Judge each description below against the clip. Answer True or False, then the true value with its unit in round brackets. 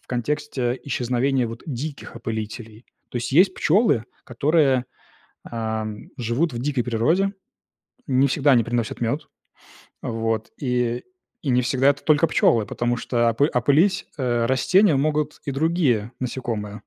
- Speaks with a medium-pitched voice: False (125 Hz)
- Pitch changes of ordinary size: True (3.8 semitones)